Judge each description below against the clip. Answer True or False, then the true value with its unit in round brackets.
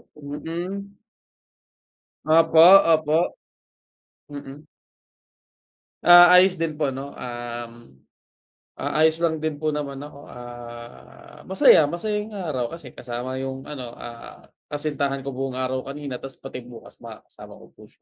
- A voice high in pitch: False (145 Hz)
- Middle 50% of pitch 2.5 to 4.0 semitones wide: True (3.7 semitones)